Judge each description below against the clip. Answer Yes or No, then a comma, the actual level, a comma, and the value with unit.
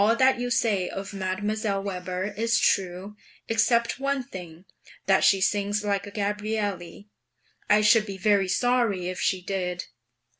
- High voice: Yes, high, 205 Hz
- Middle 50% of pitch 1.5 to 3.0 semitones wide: Yes, average, 2.7 semitones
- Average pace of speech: Yes, average, 150 wpm